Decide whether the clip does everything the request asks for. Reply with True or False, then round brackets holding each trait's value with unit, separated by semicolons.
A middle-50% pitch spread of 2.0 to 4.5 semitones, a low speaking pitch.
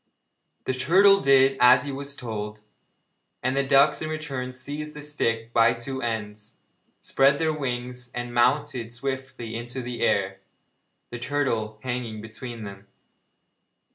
True (3.2 semitones; 125 Hz)